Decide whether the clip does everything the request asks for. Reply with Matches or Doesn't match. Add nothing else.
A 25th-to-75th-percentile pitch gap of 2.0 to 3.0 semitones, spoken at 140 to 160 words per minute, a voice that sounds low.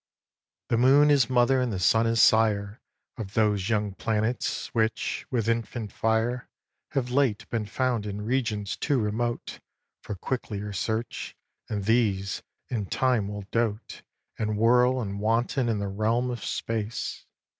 Matches